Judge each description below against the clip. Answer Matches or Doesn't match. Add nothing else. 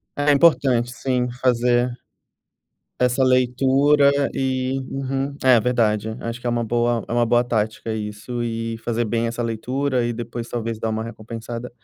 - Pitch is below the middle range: Matches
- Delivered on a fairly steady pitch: Matches